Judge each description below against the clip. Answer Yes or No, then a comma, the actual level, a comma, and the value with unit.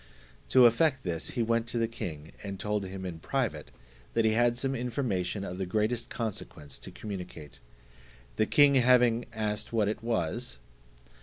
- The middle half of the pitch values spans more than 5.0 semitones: No, average, 4.2 semitones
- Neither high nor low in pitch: No, low, 110 Hz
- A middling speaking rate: Yes, average, 165 wpm